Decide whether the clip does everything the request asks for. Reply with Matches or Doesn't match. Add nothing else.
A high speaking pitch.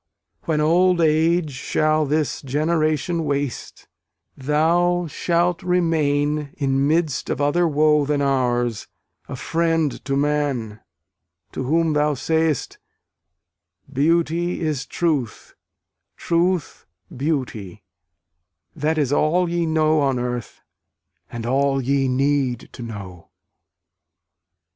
Doesn't match